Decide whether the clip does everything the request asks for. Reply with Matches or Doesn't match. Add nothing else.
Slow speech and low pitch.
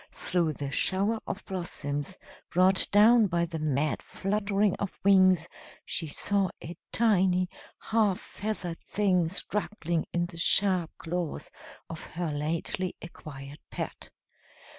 Doesn't match